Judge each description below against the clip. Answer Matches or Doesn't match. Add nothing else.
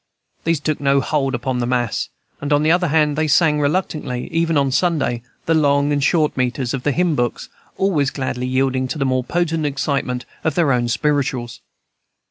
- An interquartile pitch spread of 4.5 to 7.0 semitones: Doesn't match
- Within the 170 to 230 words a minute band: Matches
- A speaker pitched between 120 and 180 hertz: Matches